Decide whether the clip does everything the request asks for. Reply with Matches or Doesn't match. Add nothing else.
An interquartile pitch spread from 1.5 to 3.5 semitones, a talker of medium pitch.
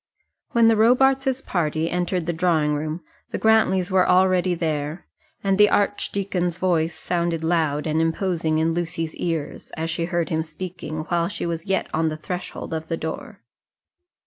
Matches